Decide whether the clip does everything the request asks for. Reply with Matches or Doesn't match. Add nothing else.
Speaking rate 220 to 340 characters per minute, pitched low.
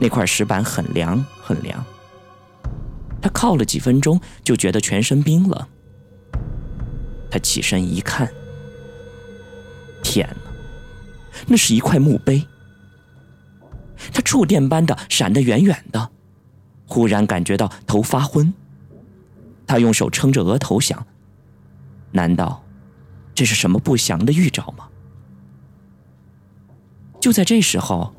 Doesn't match